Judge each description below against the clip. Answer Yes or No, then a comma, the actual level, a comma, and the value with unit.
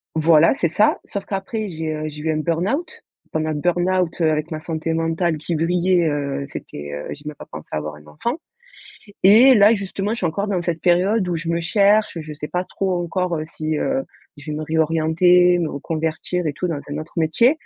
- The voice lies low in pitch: No, medium, 165 Hz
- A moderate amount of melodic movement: Yes, average, 3.0 semitones